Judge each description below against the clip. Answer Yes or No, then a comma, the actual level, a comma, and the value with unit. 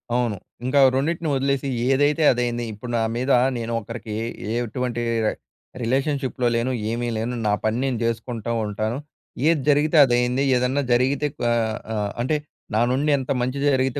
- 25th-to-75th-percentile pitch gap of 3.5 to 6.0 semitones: No, average, 2.7 semitones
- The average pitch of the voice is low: Yes, low, 125 Hz